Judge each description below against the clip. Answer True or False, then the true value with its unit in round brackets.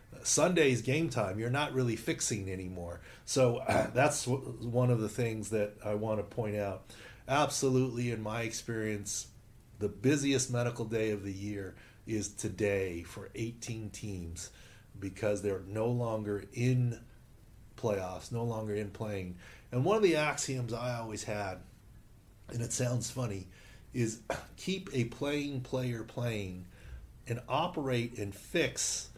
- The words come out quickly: False (140 wpm)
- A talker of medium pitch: False (115 Hz)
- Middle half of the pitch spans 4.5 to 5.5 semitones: False (3.2 semitones)